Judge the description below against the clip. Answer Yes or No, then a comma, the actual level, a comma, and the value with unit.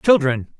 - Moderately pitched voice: Yes, medium, 155 Hz